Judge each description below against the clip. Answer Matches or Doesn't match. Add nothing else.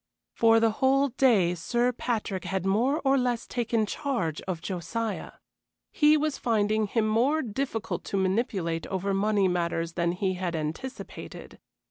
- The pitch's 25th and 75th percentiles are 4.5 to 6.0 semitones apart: Matches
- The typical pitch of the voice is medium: Doesn't match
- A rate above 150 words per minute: Doesn't match